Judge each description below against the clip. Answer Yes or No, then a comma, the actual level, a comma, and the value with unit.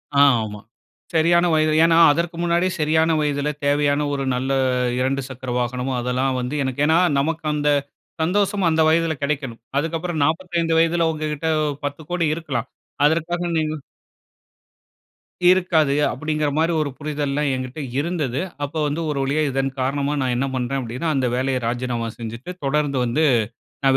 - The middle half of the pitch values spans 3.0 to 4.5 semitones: Yes, average, 3.5 semitones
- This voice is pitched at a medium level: Yes, medium, 150 Hz